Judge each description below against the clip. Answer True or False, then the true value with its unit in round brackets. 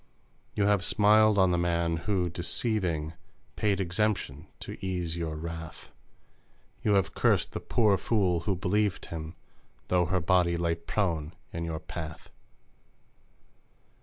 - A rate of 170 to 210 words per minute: False (135 wpm)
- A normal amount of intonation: True (3.2 semitones)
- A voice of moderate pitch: False (90 Hz)